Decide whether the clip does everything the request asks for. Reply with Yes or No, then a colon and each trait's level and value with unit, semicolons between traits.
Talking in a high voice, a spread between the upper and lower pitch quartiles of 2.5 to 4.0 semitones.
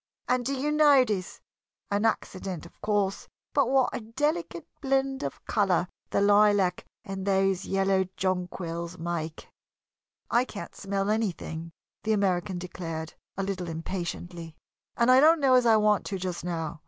No: high, 195 Hz; average, 4.9 semitones